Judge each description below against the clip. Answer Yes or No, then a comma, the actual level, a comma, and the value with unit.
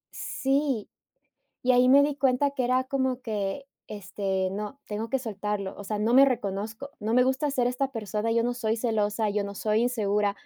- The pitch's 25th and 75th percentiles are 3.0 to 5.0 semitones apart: Yes, average, 3.8 semitones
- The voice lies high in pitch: Yes, high, 230 Hz